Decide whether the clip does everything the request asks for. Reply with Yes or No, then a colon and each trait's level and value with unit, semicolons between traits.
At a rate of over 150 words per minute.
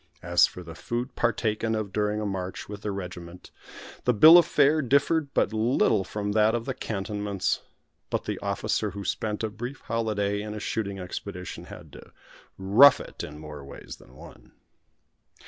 Yes: average, 175 wpm